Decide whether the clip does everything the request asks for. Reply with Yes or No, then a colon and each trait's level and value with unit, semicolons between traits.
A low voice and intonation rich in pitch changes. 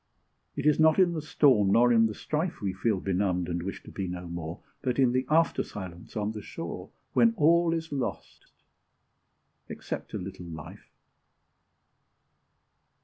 Yes: low, 110 Hz; wide, 8.7 semitones